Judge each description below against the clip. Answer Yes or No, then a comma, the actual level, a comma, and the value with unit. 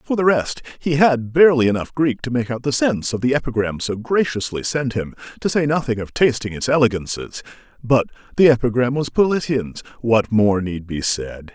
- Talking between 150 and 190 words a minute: Yes, average, 185 wpm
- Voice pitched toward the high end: No, low, 125 Hz